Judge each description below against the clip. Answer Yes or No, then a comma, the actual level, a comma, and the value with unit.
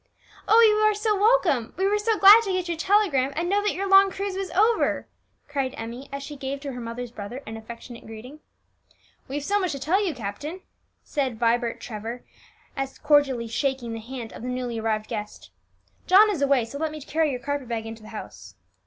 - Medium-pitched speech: No, very high, 280 Hz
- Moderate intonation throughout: No, wide, 8.3 semitones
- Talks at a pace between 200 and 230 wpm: Yes, fast, 205 wpm